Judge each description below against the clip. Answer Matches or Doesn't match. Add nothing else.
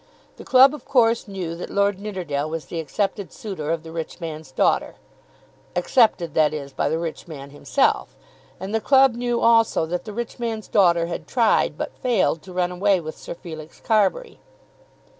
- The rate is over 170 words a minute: Matches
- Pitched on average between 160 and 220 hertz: Matches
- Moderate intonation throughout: Doesn't match